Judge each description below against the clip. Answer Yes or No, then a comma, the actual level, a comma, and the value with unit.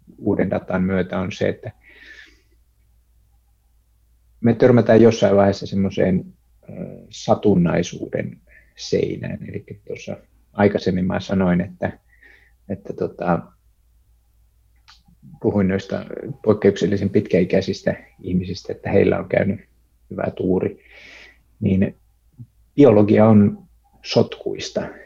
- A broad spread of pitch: No, average, 4.5 semitones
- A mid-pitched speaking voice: No, very low, 95 Hz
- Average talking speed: No, slow, 85 wpm